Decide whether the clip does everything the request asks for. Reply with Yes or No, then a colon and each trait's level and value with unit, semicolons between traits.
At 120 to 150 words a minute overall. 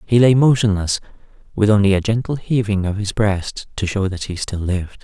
No: fast, 205 wpm